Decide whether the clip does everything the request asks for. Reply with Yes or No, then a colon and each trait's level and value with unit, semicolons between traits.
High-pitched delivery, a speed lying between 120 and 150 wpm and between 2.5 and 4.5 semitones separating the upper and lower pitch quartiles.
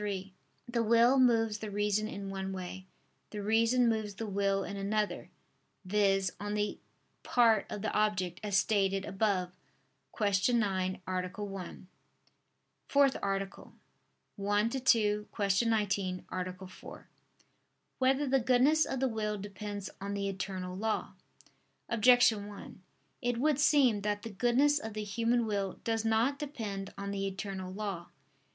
Yes: high, 210 Hz; average, 145 wpm; average, 2.8 semitones